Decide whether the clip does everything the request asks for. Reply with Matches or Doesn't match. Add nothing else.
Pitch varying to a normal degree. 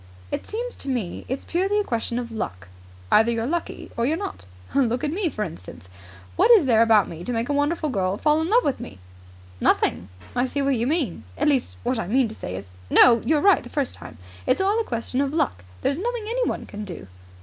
Doesn't match